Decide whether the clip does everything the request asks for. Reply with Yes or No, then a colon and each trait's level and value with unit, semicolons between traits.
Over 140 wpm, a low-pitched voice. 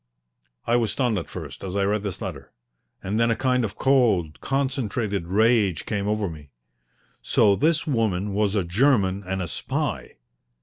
Yes: average, 170 wpm; low, 105 Hz